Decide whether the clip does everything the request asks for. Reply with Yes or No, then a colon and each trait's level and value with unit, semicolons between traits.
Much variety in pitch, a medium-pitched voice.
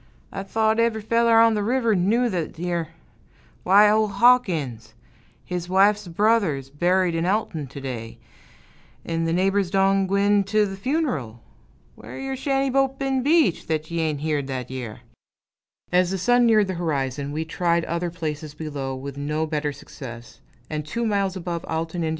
Yes: wide, 5.9 semitones; medium, 180 Hz